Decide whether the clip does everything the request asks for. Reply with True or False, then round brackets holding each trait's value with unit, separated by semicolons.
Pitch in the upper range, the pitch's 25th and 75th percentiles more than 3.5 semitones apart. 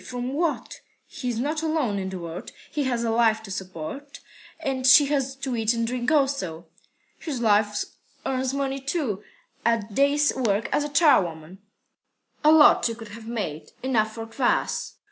True (240 Hz; 4.7 semitones)